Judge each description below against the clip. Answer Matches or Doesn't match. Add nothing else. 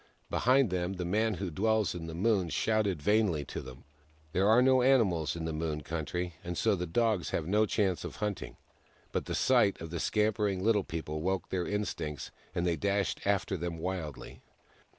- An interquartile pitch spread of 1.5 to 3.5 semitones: Doesn't match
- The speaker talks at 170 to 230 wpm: Matches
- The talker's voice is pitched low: Matches